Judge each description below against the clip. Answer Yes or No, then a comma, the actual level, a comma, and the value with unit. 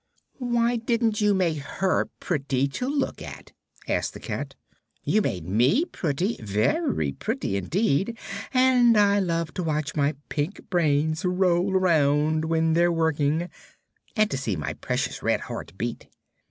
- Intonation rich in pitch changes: Yes, wide, 6.5 semitones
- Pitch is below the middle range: No, medium, 170 Hz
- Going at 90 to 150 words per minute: Yes, average, 145 wpm